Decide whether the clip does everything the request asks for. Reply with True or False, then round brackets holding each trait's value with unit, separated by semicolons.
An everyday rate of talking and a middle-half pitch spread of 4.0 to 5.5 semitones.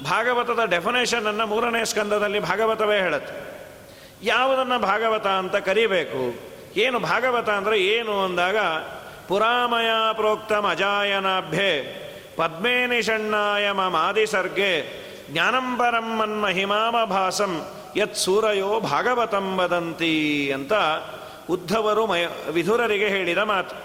False (85 wpm; 3.4 semitones)